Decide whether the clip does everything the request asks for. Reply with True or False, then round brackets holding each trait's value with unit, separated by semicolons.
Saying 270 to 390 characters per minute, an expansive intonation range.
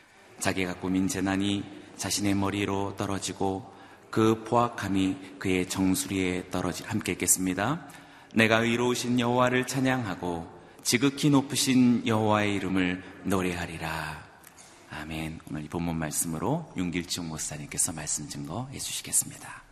False (310 characters per minute; 4.9 semitones)